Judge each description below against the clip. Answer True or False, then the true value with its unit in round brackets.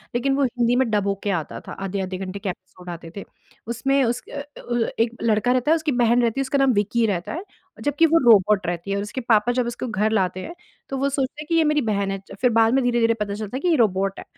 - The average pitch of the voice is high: True (230 Hz)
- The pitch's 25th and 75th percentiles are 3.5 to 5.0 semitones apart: True (4.7 semitones)